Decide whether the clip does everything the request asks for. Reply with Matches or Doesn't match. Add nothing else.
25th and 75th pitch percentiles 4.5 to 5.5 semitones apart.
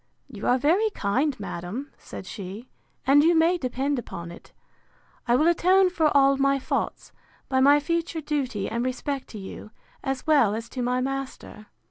Doesn't match